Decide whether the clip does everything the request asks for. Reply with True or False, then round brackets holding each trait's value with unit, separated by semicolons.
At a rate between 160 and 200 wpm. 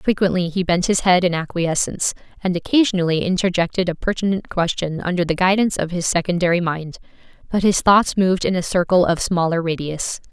True (175 wpm)